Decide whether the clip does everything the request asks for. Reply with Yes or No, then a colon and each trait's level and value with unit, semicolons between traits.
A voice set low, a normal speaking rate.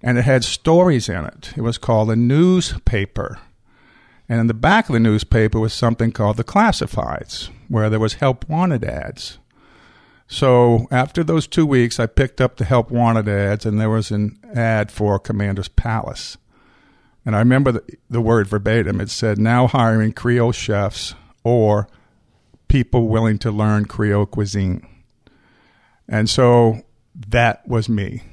Yes: low, 115 Hz; average, 155 wpm